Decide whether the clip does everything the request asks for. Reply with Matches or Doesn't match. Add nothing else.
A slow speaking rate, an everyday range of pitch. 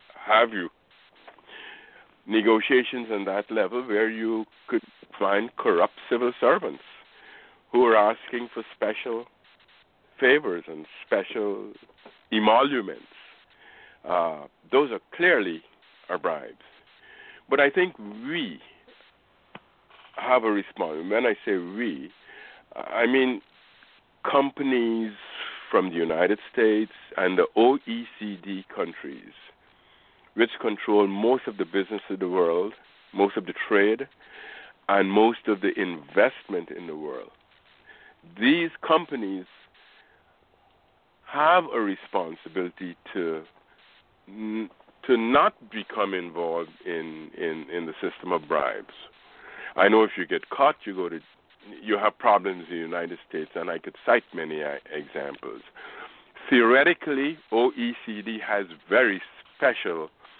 Doesn't match